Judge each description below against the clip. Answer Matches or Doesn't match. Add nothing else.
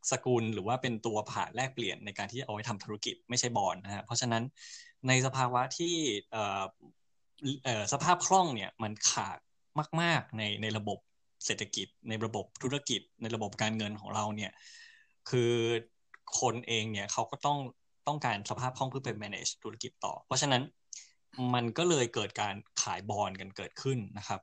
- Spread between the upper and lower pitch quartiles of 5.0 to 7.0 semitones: Doesn't match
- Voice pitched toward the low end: Matches